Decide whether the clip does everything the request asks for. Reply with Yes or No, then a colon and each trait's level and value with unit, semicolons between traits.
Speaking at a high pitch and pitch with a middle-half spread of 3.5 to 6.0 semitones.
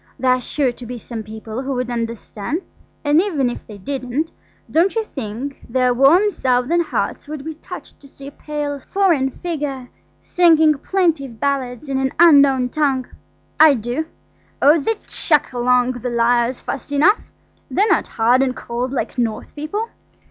Yes: very high, 270 Hz; average, 3.8 semitones